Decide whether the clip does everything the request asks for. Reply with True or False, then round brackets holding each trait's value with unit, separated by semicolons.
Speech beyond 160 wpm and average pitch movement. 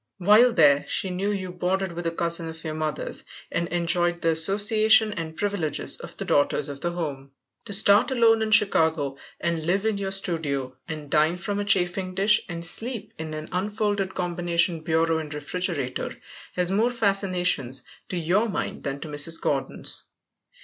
True (170 wpm; 3.9 semitones)